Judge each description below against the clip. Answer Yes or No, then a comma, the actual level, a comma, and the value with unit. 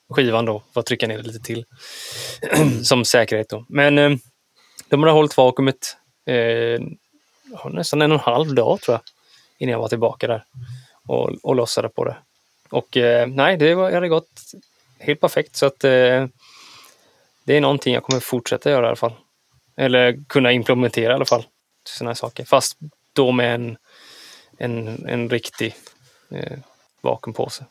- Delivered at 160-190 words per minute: Yes, average, 165 wpm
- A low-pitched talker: Yes, low, 130 Hz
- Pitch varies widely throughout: No, average, 3.3 semitones